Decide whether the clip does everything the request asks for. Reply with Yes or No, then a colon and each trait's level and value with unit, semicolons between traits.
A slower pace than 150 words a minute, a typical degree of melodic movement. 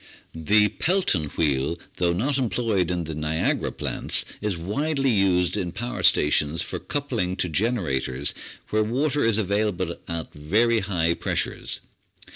No: slow, 135 wpm; wide, 5.9 semitones